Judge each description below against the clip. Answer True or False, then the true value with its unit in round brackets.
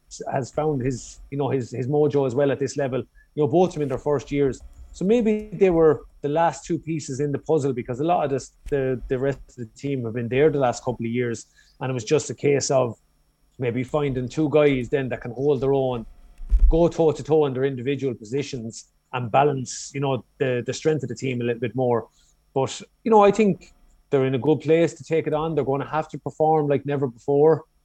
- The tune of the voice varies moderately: True (3.0 semitones)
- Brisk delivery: True (240 wpm)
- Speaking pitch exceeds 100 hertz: True (140 Hz)